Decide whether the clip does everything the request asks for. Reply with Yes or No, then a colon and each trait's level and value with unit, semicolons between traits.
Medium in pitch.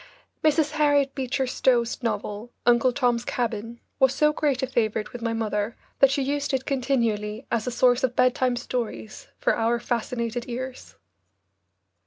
No: high, 245 Hz